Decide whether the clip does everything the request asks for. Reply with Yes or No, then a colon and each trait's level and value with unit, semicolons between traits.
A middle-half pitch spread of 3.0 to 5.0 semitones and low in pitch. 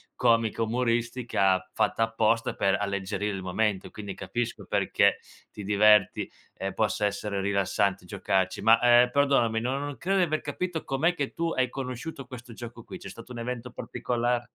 Yes: average, 3.7 semitones; low, 115 Hz